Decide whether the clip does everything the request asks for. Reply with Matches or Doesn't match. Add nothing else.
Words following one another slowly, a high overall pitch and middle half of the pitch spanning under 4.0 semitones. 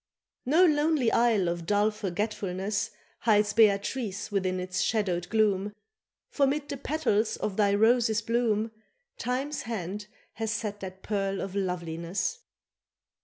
Matches